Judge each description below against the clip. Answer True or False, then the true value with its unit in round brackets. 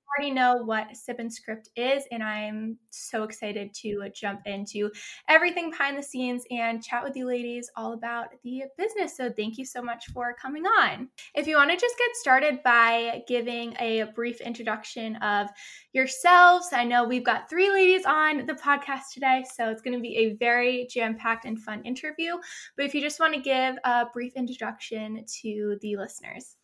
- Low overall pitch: False (245 Hz)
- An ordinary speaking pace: True (190 wpm)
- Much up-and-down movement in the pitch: False (3.8 semitones)